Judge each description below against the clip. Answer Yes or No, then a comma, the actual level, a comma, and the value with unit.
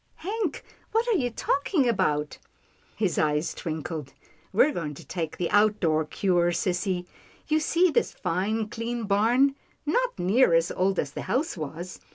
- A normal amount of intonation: No, wide, 8.1 semitones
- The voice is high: Yes, high, 200 Hz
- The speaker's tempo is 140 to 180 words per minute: Yes, average, 175 wpm